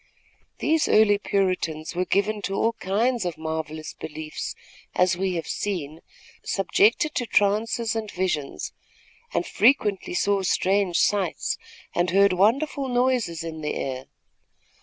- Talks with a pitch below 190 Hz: No, high, 195 Hz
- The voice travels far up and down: No, average, 4.4 semitones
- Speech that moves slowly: Yes, slow, 130 wpm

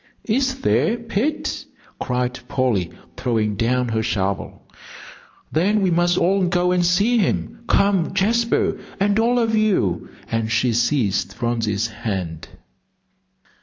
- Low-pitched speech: No, medium, 160 Hz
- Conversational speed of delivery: No, slow, 125 wpm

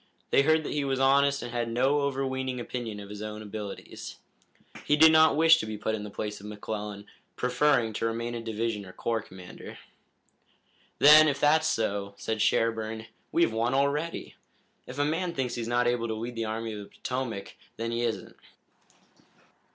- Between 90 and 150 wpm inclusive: No, average, 185 wpm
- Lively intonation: No, average, 4.3 semitones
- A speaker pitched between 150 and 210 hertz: No, low, 120 Hz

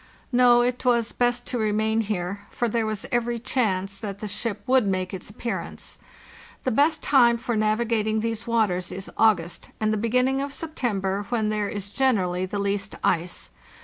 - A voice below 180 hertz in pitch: No, high, 220 Hz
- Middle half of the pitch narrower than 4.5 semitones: Yes, average, 3.3 semitones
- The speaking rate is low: No, average, 175 wpm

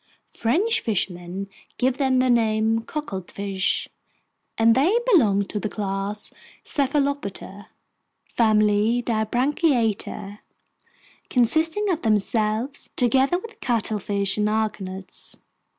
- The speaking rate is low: Yes, slow, 90 wpm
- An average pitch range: Yes, average, 4.5 semitones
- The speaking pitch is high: Yes, high, 225 Hz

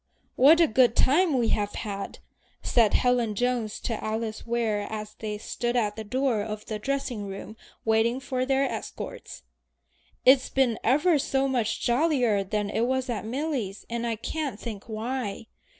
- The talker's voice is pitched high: Yes, high, 235 Hz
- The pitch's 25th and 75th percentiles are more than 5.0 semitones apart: No, average, 3.5 semitones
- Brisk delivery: No, average, 165 wpm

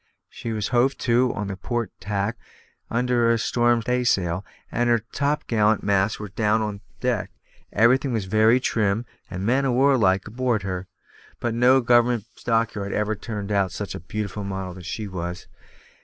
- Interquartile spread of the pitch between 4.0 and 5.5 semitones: No, average, 3.4 semitones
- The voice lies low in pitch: Yes, low, 110 Hz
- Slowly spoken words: No, average, 170 wpm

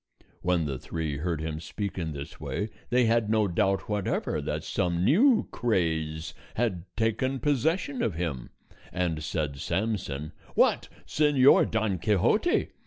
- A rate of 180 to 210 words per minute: No, average, 140 wpm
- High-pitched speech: No, very low, 95 Hz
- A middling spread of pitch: No, wide, 6.2 semitones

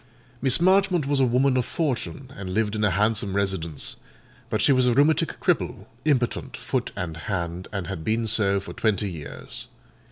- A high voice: No, low, 110 Hz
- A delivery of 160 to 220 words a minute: Yes, average, 180 wpm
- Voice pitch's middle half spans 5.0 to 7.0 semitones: Yes, wide, 5.6 semitones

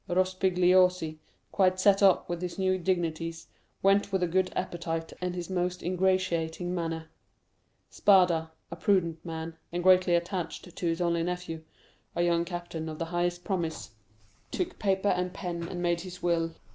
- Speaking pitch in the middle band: Yes, medium, 175 Hz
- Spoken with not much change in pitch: Yes, narrow, 1.8 semitones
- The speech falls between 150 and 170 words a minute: Yes, average, 160 wpm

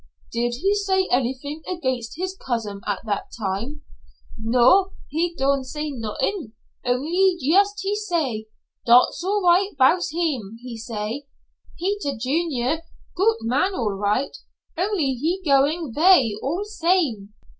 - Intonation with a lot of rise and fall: Yes, wide, 7.3 semitones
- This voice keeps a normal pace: No, slow, 130 wpm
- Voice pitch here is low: No, very high, 285 Hz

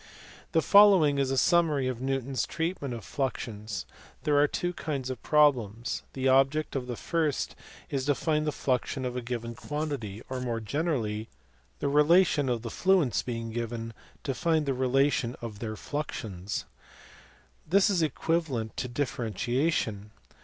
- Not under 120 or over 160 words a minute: Yes, average, 155 wpm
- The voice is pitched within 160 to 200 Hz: No, low, 135 Hz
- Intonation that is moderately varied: Yes, average, 4.3 semitones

